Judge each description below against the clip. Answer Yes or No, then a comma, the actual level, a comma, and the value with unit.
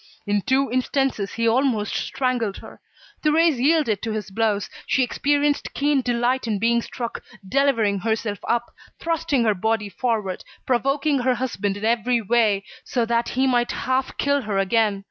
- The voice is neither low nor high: No, high, 235 Hz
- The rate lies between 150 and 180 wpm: Yes, average, 160 wpm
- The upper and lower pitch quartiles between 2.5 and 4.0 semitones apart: Yes, average, 3.7 semitones